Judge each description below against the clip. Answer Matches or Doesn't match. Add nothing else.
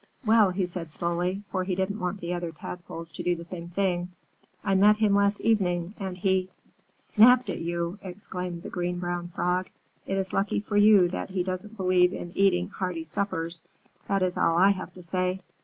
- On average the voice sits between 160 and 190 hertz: Matches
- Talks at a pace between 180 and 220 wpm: Matches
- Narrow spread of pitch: Matches